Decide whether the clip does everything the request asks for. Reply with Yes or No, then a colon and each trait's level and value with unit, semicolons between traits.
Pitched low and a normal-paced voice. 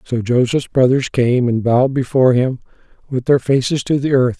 Yes: low, 130 Hz; average, 190 wpm